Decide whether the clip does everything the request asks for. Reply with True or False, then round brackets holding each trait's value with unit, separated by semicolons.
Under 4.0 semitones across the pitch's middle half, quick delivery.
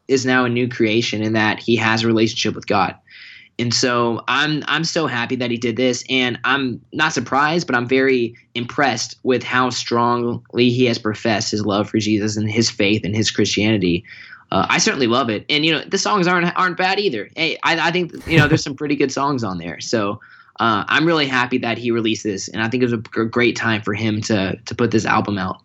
True (3.3 semitones; 230 wpm)